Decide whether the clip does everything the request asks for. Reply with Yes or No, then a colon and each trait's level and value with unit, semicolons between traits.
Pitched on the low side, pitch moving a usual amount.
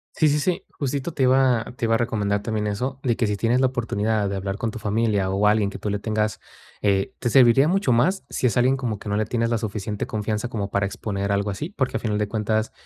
Yes: low, 110 Hz; average, 3.5 semitones